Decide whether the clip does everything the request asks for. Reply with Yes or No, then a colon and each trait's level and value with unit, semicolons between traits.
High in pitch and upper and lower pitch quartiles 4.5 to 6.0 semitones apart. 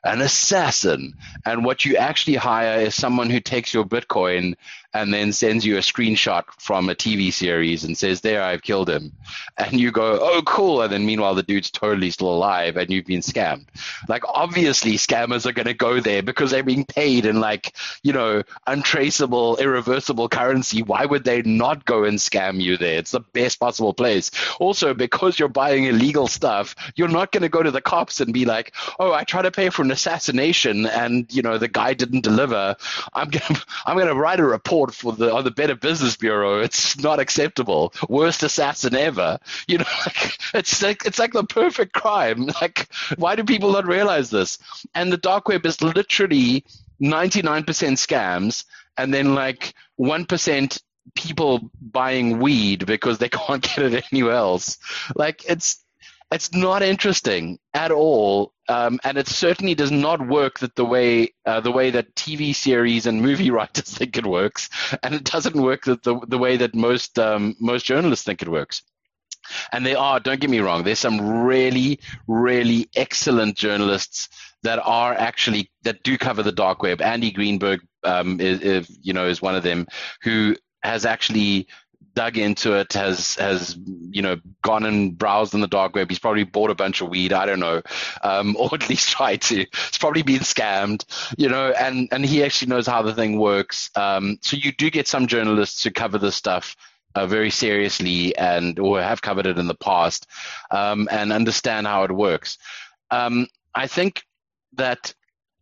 No: low, 120 Hz; average, 5.1 semitones